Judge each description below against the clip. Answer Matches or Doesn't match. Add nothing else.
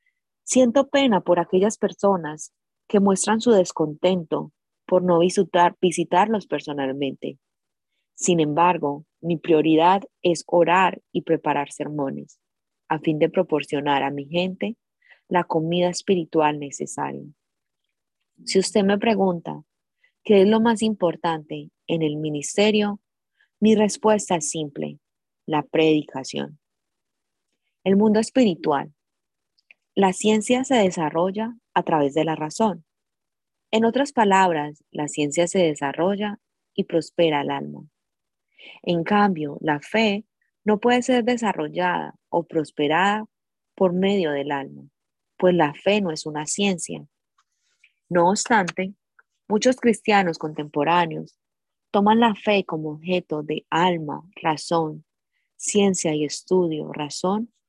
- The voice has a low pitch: Doesn't match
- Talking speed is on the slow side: Matches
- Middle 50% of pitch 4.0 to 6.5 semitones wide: Matches